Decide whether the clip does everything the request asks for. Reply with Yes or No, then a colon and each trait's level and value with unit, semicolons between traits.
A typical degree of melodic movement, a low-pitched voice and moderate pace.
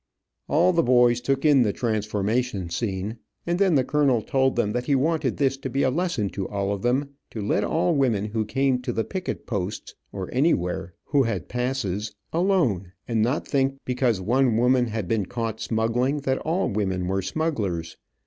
Yes: average, 4.8 semitones; low, 120 Hz; average, 185 wpm